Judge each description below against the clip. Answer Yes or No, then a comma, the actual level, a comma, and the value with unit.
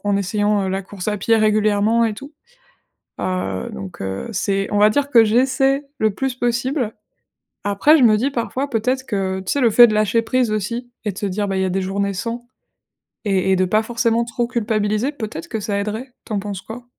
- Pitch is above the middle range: Yes, high, 215 Hz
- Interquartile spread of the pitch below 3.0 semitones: No, average, 3.3 semitones